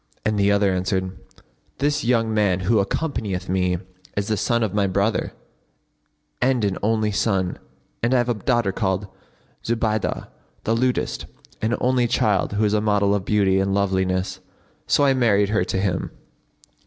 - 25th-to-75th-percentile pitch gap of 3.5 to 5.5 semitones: No, average, 3.0 semitones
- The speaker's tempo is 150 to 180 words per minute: Yes, average, 165 wpm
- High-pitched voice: No, low, 105 Hz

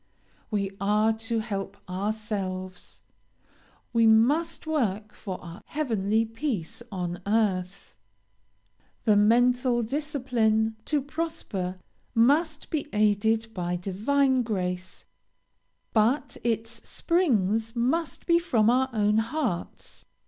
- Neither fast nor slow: No, slow, 100 wpm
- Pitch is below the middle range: No, high, 225 Hz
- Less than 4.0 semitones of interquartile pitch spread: No, average, 4.3 semitones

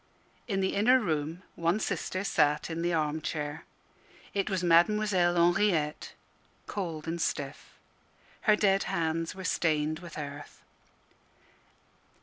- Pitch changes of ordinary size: Yes, average, 3.7 semitones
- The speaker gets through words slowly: Yes, slow, 125 wpm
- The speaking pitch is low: No, medium, 170 Hz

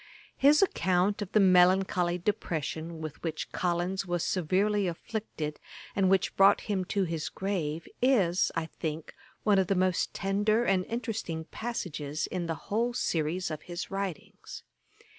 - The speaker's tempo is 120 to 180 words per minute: Yes, average, 145 wpm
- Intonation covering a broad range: No, average, 3.3 semitones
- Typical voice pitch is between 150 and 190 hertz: Yes, medium, 185 Hz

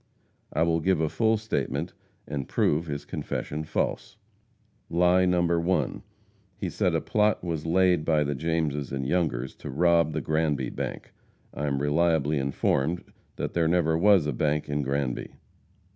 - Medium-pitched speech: No, very low, 80 Hz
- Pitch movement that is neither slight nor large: Yes, average, 3.1 semitones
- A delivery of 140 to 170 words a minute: Yes, average, 160 wpm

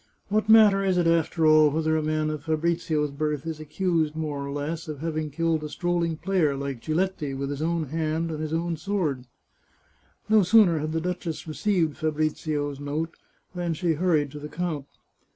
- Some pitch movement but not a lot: No, narrow, 2.2 semitones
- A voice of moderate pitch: Yes, medium, 160 Hz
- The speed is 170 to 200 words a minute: Yes, average, 190 wpm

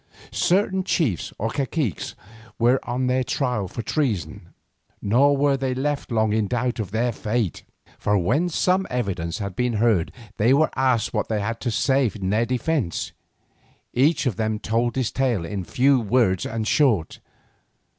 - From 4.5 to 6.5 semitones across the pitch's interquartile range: No, average, 4.0 semitones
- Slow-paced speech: No, average, 165 wpm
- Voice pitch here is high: No, low, 120 Hz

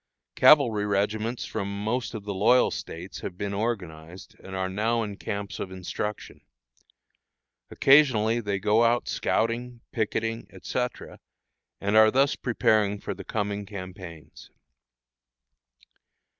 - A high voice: No, low, 105 Hz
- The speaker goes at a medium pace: No, slow, 120 wpm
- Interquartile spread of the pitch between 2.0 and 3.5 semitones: Yes, average, 2.8 semitones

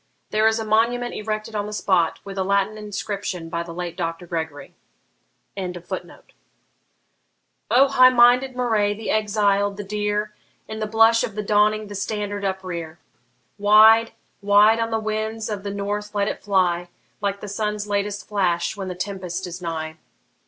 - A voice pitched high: Yes, high, 205 Hz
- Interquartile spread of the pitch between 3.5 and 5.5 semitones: No, narrow, 2.4 semitones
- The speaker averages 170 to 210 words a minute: No, average, 160 wpm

